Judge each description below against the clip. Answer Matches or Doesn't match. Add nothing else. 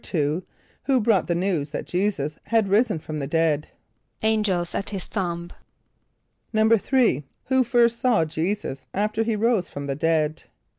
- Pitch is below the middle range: Doesn't match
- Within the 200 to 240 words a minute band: Doesn't match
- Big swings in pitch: Matches